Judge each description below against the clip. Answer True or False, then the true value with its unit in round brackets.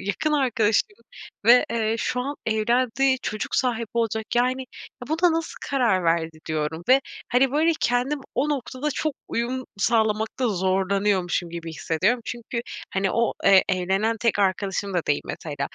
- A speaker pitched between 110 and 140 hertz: False (225 Hz)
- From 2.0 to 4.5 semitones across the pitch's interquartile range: False (5.0 semitones)